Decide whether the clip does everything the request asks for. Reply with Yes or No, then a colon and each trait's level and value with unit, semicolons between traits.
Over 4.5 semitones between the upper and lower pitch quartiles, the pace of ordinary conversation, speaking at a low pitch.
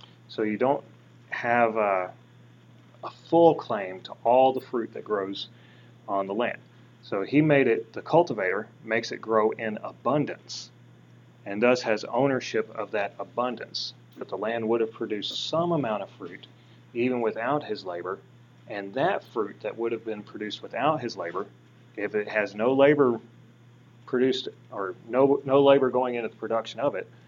Yes: average, 5.1 semitones; average, 165 wpm; low, 110 Hz